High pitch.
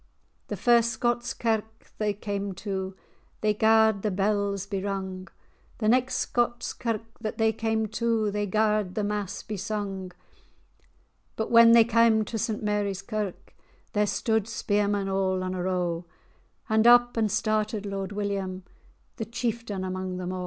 Yes: high, 210 Hz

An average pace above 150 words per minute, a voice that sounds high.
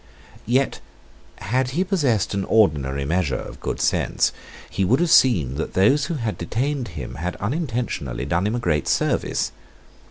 No: average, 160 wpm; low, 110 Hz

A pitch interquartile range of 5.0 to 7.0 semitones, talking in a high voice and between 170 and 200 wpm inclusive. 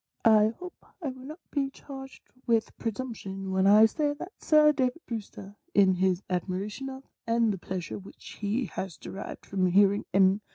Yes: wide, 5.6 semitones; high, 215 Hz; average, 175 wpm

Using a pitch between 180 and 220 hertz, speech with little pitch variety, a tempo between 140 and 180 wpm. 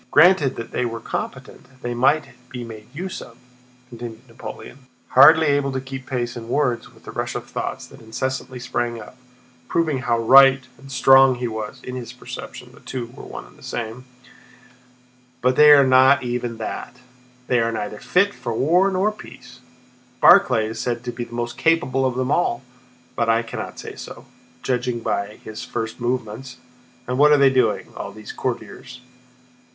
No: low, 125 Hz; narrow, 2.2 semitones; average, 175 wpm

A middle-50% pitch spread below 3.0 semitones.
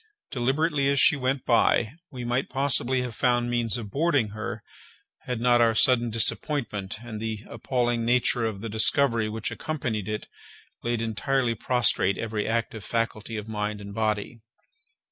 Yes: narrow, 2.6 semitones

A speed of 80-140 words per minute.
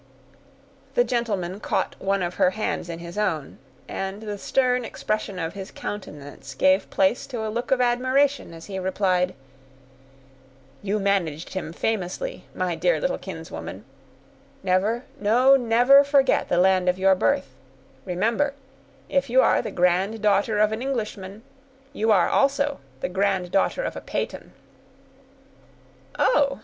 Yes: slow, 135 wpm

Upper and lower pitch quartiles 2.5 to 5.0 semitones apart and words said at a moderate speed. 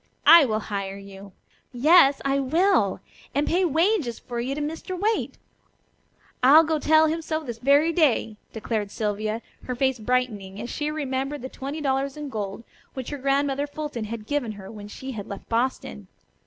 No: wide, 5.4 semitones; average, 175 wpm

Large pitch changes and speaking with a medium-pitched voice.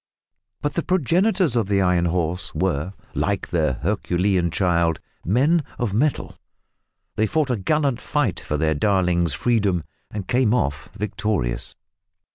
No: wide, 6.4 semitones; low, 100 Hz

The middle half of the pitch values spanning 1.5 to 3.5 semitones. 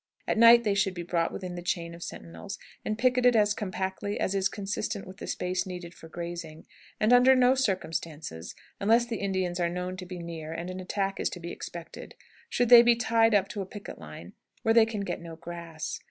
No: average, 4.2 semitones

